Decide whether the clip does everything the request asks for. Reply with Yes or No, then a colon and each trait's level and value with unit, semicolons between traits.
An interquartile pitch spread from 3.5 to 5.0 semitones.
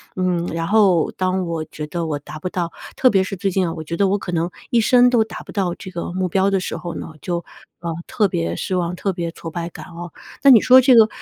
No: average, 2.8 semitones